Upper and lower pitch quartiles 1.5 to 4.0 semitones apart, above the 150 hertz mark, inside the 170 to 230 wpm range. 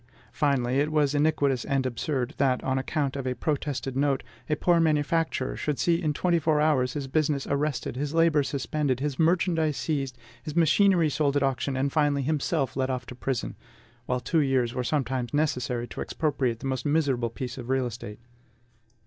No: average, 2.9 semitones; medium, 140 Hz; average, 185 wpm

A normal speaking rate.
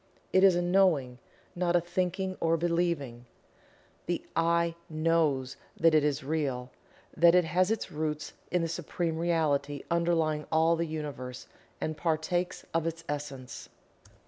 Yes: average, 145 wpm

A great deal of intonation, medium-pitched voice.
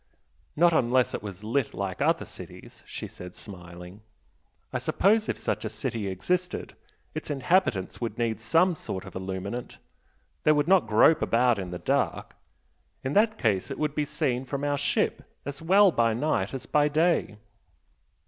No: wide, 7.3 semitones; low, 130 Hz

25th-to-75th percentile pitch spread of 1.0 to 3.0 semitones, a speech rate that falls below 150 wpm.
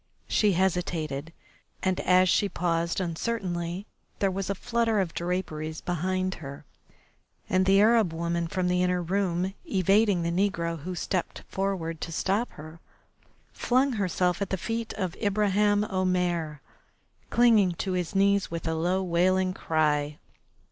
Yes: average, 2.7 semitones; average, 140 wpm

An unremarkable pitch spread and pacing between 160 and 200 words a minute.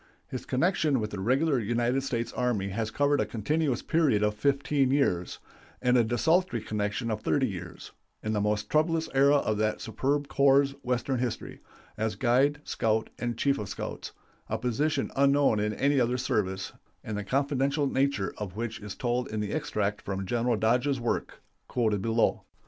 Yes: average, 4.5 semitones; average, 170 wpm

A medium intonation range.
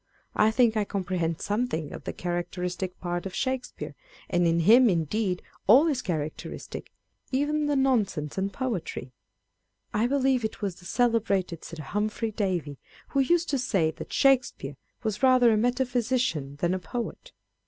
No: wide, 6.1 semitones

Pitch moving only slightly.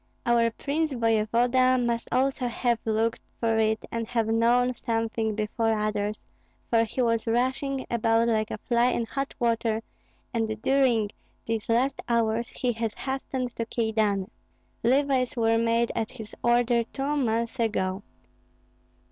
Yes: narrow, 1.8 semitones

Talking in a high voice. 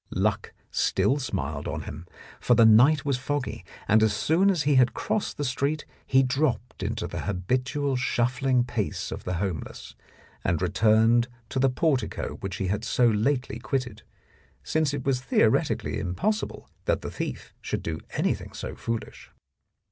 No: low, 125 Hz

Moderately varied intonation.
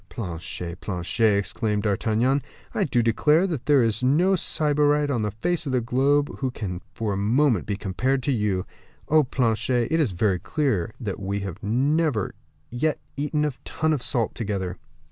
No: wide, 6.1 semitones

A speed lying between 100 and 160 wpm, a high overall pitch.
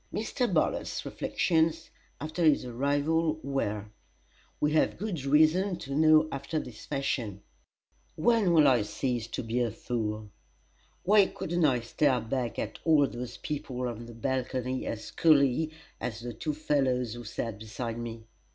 No: average, 150 wpm; low, 135 Hz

